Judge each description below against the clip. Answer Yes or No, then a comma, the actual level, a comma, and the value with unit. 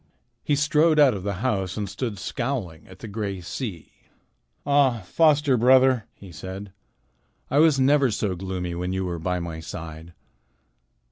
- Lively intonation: Yes, wide, 6.6 semitones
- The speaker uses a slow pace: No, average, 155 wpm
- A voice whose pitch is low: Yes, low, 105 Hz